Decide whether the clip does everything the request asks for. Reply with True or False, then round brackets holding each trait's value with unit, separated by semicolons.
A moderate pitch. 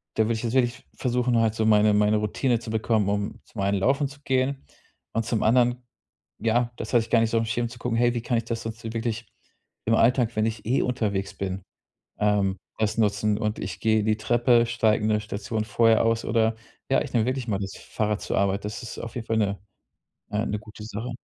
False (110 Hz)